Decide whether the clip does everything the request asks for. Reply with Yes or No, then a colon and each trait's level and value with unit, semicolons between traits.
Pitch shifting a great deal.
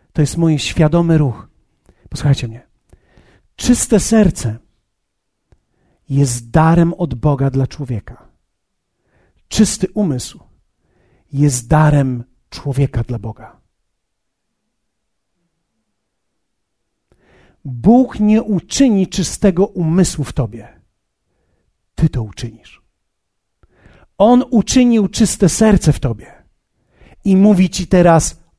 Yes: wide, 8.0 semitones